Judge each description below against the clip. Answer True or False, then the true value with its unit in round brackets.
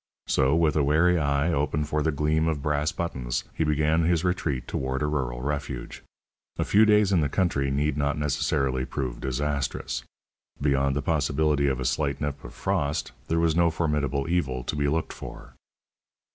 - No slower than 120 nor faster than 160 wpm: False (180 wpm)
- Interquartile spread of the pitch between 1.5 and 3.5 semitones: True (2.6 semitones)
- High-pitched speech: False (75 Hz)